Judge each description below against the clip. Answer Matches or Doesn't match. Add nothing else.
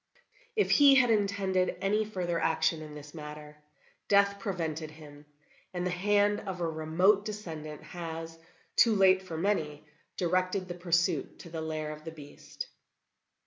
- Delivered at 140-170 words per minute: Matches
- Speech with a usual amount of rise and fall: Matches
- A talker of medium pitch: Matches